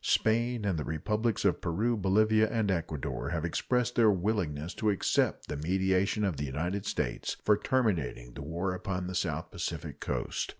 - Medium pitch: No, very low, 95 Hz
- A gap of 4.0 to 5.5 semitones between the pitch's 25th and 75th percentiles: Yes, average, 4.8 semitones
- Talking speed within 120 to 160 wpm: No, average, 170 wpm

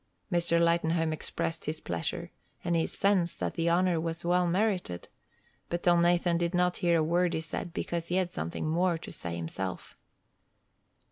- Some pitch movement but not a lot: No, narrow, 1.5 semitones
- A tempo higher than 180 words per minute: No, average, 165 wpm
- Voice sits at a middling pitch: Yes, medium, 170 Hz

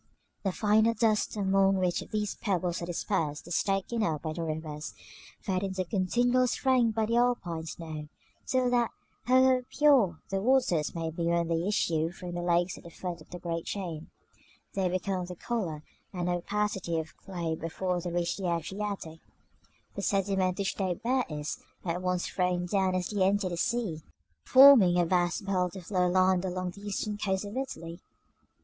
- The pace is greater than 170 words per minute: Yes, average, 180 wpm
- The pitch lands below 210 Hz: Yes, medium, 185 Hz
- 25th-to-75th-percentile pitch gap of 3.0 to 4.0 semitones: Yes, average, 3.4 semitones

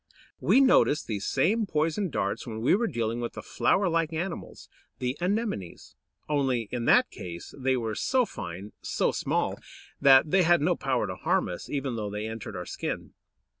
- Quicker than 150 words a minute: Yes, average, 180 wpm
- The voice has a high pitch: No, low, 135 Hz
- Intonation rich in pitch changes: Yes, wide, 7.6 semitones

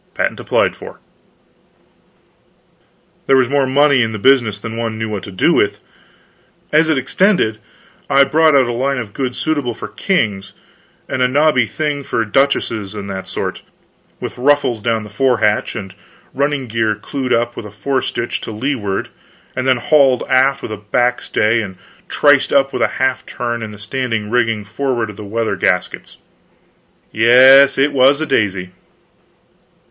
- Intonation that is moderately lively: Yes, average, 4.2 semitones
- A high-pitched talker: No, low, 125 Hz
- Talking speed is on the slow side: No, average, 170 wpm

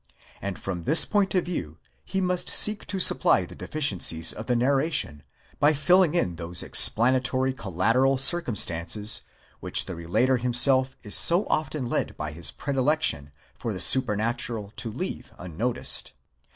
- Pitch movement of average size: No, wide, 8.2 semitones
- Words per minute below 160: Yes, average, 145 wpm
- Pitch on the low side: Yes, low, 125 Hz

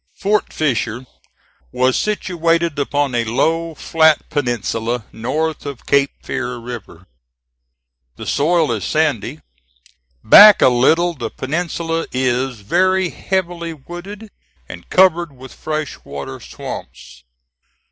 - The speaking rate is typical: No, slow, 110 wpm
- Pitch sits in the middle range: Yes, medium, 150 Hz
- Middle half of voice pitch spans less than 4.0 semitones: No, wide, 5.6 semitones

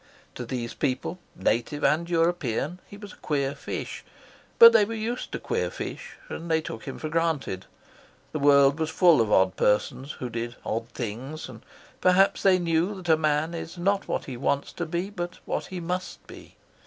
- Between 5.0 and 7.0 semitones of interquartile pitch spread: Yes, wide, 5.4 semitones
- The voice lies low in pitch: No, medium, 155 Hz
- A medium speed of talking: Yes, average, 190 wpm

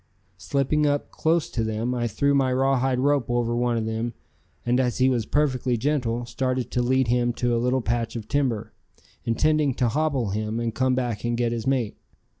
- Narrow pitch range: Yes, narrow, 2.3 semitones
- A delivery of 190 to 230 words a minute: Yes, average, 200 wpm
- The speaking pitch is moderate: No, low, 125 Hz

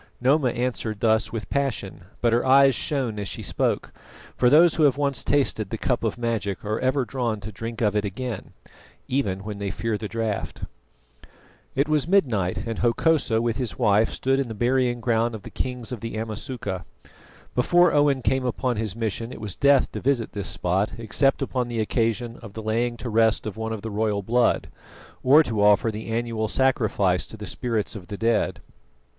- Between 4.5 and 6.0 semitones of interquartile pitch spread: No, average, 3.1 semitones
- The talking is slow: No, average, 195 wpm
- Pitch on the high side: No, low, 115 Hz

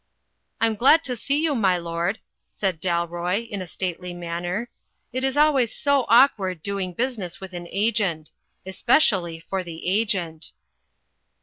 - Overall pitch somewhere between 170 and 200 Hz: Yes, high, 190 Hz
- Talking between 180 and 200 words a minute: No, average, 150 wpm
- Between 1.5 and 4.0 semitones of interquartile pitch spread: No, average, 5.2 semitones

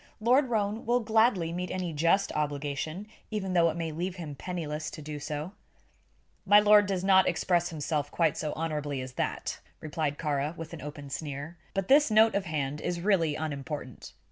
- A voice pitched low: No, medium, 165 Hz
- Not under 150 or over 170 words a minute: No, average, 180 wpm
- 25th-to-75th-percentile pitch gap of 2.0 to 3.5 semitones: No, average, 4.4 semitones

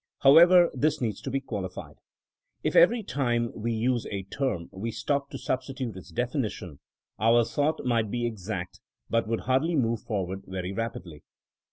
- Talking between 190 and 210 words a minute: No, average, 170 wpm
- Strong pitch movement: No, average, 4.6 semitones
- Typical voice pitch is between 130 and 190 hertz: No, low, 115 Hz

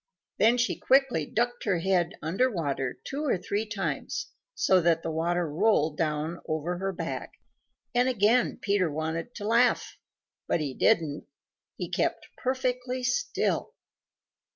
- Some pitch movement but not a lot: No, wide, 7.0 semitones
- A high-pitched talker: Yes, high, 195 Hz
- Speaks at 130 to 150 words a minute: Yes, average, 140 wpm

